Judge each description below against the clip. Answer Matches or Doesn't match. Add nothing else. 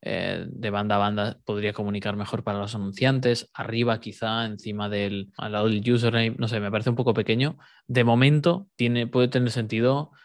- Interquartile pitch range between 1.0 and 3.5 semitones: Matches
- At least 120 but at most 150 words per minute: Doesn't match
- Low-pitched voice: Matches